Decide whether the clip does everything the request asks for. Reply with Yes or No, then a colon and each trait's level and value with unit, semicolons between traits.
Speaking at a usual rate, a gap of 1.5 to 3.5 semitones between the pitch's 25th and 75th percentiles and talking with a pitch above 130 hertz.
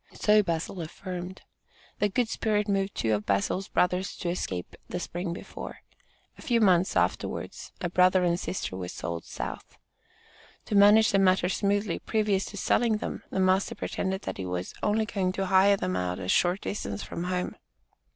Yes: average, 175 wpm; average, 2.8 semitones; medium, 185 Hz